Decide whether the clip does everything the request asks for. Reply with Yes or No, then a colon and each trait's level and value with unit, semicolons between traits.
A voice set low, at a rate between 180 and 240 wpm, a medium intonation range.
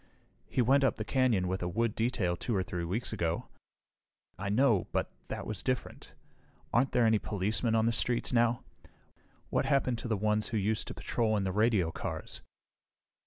Yes: low, 110 Hz; average, 185 wpm; average, 3.5 semitones